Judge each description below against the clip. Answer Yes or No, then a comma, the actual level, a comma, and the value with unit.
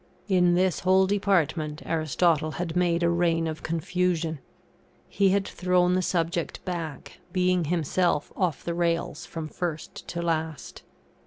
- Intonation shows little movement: Yes, narrow, 2.1 semitones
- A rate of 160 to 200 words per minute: No, average, 140 wpm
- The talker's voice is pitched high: No, medium, 170 Hz